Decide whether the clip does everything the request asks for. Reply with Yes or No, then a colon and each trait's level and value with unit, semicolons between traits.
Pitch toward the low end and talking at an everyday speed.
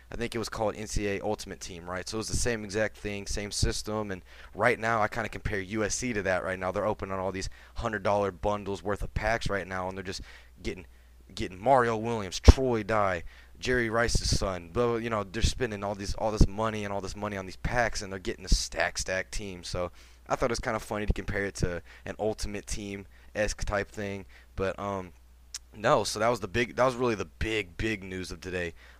No: low, 100 Hz; fast, 230 wpm